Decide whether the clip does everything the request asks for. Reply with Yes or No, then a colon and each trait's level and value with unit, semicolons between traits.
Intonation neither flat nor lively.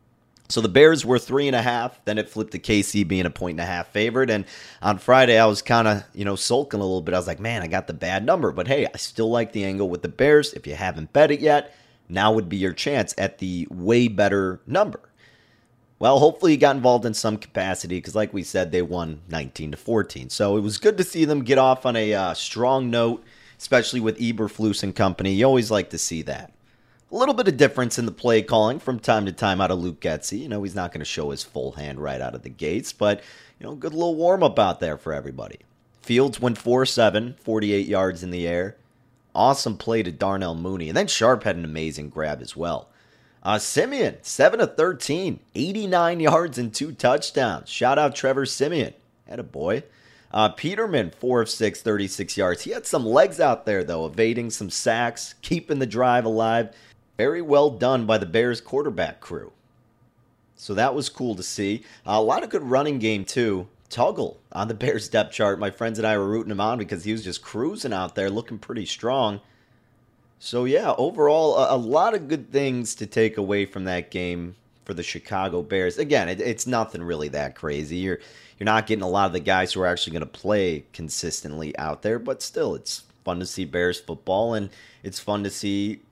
Yes: average, 4.3 semitones